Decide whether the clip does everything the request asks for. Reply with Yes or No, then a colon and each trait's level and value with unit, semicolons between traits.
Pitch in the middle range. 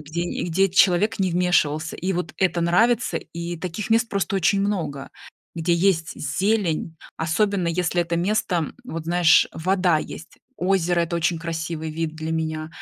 Yes: medium, 170 Hz